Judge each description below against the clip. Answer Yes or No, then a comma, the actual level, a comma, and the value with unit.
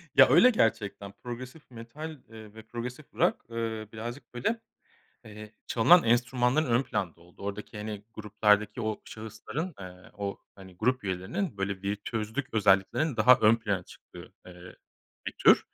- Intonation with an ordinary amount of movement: Yes, average, 3.4 semitones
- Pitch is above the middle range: No, low, 110 Hz